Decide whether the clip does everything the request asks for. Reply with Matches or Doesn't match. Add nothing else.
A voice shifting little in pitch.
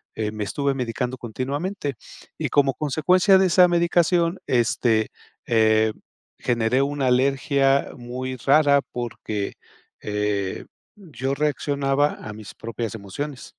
Doesn't match